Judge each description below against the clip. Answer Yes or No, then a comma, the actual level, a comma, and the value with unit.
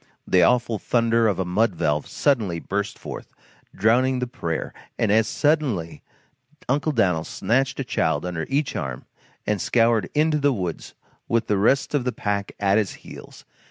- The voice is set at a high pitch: No, low, 110 Hz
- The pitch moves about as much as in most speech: No, wide, 5.7 semitones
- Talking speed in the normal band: Yes, average, 165 wpm